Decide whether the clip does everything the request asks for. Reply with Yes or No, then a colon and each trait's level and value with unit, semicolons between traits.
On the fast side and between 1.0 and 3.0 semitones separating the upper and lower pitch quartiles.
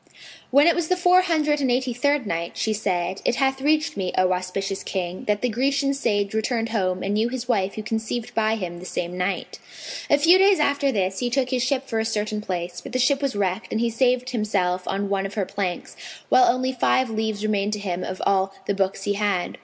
No: fast, 230 wpm; average, 5.1 semitones